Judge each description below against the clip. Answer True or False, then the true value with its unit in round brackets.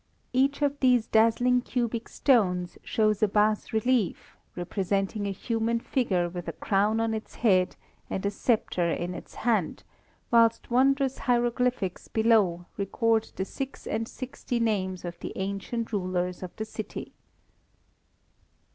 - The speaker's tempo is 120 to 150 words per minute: True (140 wpm)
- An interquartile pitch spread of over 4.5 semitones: False (4.0 semitones)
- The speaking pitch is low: False (220 Hz)